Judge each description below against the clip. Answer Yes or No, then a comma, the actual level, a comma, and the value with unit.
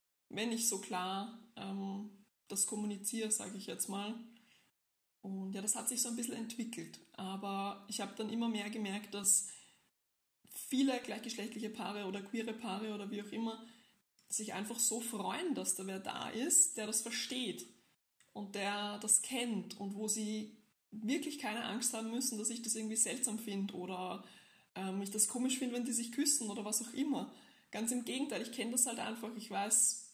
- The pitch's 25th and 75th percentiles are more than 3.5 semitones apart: No, narrow, 2.6 semitones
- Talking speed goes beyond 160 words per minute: Yes, average, 185 wpm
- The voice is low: No, high, 220 Hz